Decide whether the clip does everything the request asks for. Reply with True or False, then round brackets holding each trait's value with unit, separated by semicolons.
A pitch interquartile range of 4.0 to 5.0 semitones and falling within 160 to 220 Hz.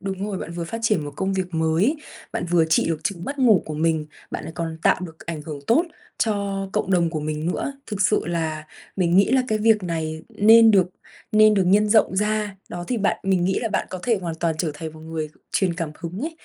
True (4.5 semitones; 185 Hz)